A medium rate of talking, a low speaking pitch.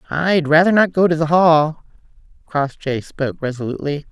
No: average, 145 wpm; medium, 155 Hz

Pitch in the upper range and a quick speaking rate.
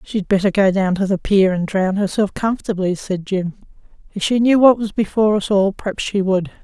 Yes: high, 200 Hz; fast, 215 wpm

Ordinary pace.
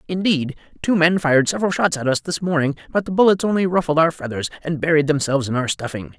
No: fast, 225 wpm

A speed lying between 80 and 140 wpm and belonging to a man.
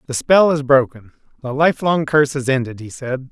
No: average, 200 wpm; male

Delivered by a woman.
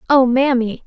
Yes: female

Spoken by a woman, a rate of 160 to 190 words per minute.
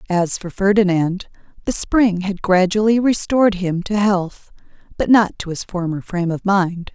Yes: female; average, 165 wpm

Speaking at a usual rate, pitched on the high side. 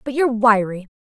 Yes: average, 175 wpm; high, 230 Hz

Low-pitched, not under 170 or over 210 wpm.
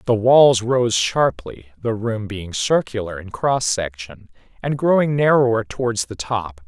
No: low, 115 Hz; average, 155 wpm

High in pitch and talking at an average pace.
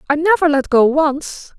Yes: very high, 300 Hz; average, 190 wpm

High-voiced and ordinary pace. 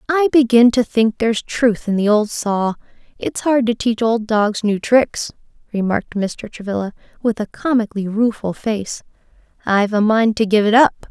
Yes: high, 220 Hz; average, 180 wpm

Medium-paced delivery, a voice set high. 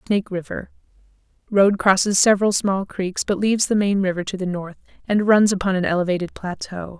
Yes: average, 170 wpm; high, 195 Hz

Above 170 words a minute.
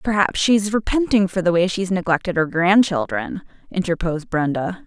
No: average, 160 wpm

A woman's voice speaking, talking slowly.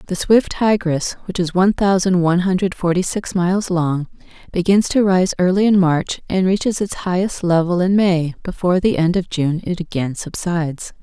No: female; average, 185 wpm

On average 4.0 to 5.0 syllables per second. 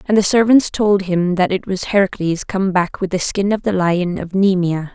Yes: 4.8 syllables/s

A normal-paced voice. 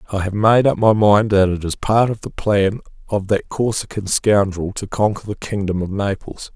No: fast, 210 wpm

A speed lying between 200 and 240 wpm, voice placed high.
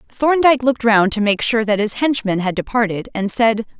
Yes: fast, 205 wpm; high, 225 Hz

